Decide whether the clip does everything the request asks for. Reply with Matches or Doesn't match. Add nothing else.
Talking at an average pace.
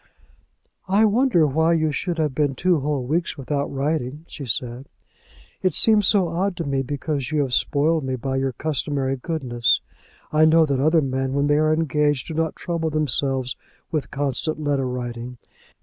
Matches